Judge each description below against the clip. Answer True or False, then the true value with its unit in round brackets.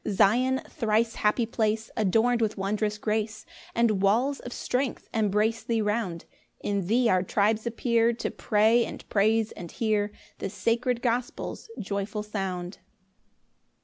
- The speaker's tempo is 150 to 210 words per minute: False (140 wpm)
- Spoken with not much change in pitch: True (2.2 semitones)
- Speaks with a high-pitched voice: True (220 Hz)